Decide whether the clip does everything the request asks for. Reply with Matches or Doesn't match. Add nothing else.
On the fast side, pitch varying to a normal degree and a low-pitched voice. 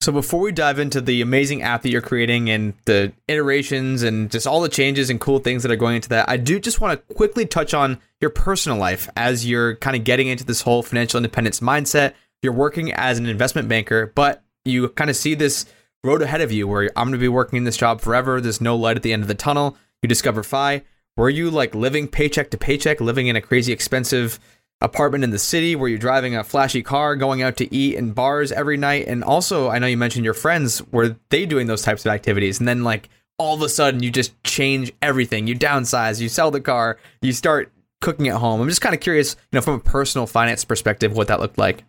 Matches